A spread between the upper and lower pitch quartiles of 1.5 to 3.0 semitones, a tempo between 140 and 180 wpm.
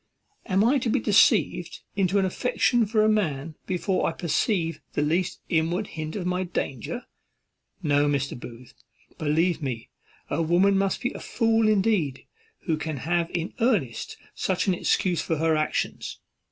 No: average, 4.4 semitones; average, 160 wpm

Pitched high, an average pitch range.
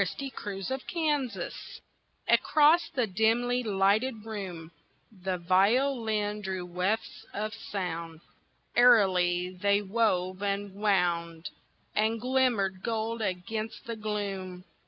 Yes: high, 205 Hz; average, 3.6 semitones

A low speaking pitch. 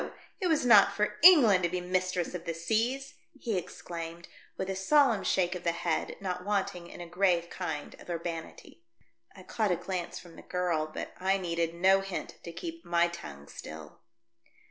No: medium, 180 Hz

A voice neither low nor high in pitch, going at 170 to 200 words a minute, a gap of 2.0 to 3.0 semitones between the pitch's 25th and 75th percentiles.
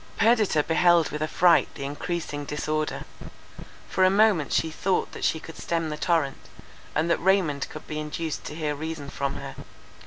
Yes: medium, 160 Hz; average, 175 wpm; narrow, 2.5 semitones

